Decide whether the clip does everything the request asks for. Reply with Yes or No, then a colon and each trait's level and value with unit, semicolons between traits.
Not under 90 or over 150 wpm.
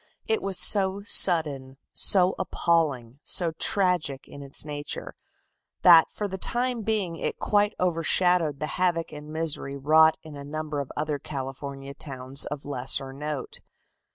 Yes: average, 145 wpm